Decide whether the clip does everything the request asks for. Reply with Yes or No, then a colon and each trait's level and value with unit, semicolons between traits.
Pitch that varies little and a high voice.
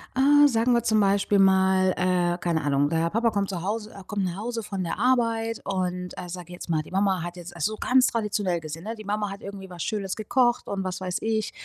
No: average, 3.3 semitones; high, 195 Hz